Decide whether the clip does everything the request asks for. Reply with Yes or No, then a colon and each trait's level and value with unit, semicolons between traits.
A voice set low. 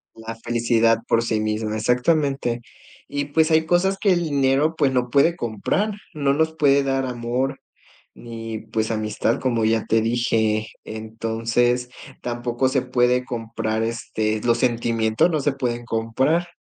Yes: low, 120 Hz